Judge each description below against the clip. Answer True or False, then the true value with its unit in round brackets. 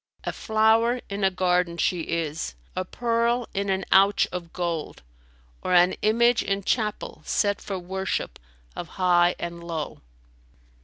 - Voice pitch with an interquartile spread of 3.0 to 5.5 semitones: True (3.5 semitones)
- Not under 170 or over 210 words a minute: False (150 wpm)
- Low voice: False (185 Hz)